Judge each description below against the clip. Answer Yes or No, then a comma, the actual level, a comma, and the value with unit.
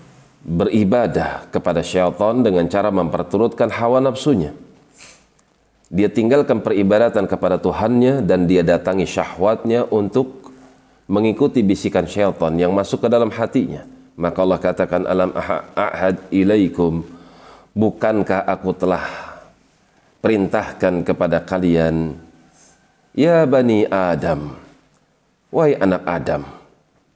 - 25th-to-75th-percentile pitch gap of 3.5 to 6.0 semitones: Yes, average, 3.8 semitones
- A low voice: Yes, very low, 95 Hz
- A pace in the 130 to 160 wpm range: No, average, 95 wpm